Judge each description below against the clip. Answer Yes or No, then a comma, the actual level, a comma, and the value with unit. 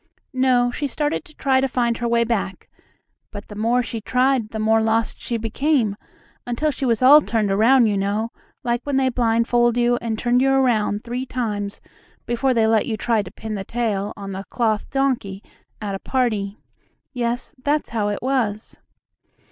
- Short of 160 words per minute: No, average, 185 wpm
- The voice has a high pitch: Yes, high, 235 Hz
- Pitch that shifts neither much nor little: Yes, average, 3.0 semitones